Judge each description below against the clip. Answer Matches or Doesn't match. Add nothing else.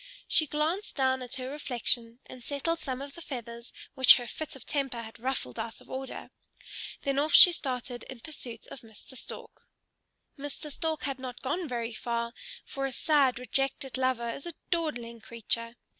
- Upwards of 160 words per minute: Matches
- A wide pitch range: Doesn't match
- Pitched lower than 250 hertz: Doesn't match